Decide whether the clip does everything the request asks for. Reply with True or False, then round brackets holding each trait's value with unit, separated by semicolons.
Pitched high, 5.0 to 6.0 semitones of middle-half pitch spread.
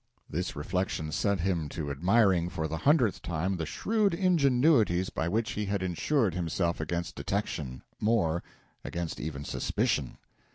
False (90 Hz; 5.4 semitones)